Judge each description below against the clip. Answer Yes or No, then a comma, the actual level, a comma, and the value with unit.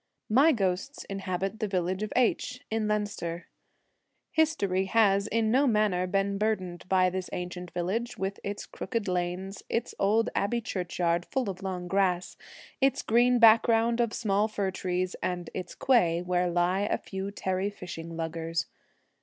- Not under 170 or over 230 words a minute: No, average, 155 wpm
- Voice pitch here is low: No, high, 195 Hz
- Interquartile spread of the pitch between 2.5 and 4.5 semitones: Yes, average, 3.5 semitones